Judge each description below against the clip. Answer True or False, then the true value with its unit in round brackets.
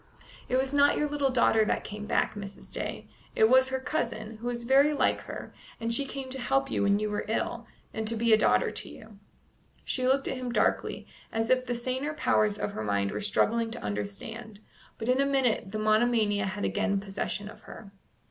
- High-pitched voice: True (225 Hz)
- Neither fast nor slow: False (215 wpm)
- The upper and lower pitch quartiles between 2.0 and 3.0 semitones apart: False (3.9 semitones)